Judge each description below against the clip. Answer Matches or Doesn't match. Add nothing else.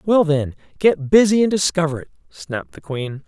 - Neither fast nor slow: Matches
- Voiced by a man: Matches